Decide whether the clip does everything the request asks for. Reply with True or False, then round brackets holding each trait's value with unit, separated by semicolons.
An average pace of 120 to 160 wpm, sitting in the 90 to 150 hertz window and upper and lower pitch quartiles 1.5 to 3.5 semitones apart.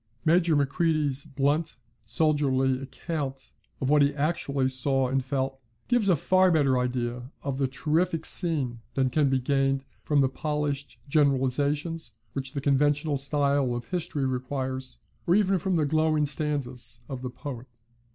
True (150 wpm; 140 Hz; 2.7 semitones)